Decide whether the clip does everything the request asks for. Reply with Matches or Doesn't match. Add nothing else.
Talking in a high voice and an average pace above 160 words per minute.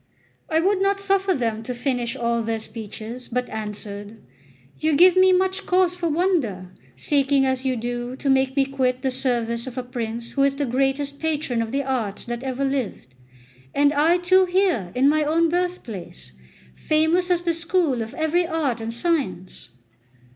Matches